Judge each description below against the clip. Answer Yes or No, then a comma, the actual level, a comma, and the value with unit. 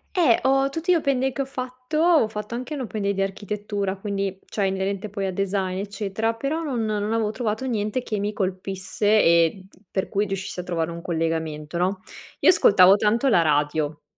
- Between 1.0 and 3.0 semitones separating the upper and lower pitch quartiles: No, average, 3.8 semitones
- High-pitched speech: Yes, high, 205 Hz